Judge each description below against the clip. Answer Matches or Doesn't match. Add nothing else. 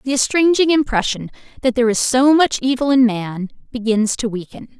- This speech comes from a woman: Matches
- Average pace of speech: Matches